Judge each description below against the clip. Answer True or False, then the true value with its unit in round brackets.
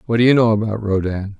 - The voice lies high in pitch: False (105 Hz)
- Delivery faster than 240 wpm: True (260 wpm)